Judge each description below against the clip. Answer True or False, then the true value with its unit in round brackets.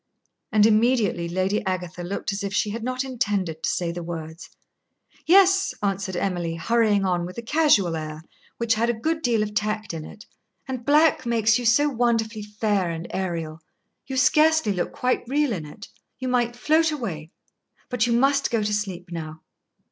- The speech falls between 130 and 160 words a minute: False (180 wpm)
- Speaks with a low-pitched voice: False (215 Hz)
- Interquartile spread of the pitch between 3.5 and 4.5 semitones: False (5.6 semitones)